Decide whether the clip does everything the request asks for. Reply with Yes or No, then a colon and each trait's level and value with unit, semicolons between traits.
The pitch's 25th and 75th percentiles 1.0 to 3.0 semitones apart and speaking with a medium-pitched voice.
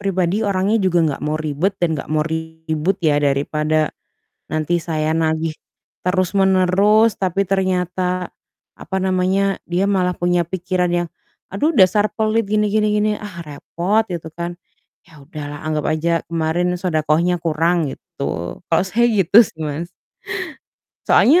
No: average, 3.4 semitones; medium, 175 Hz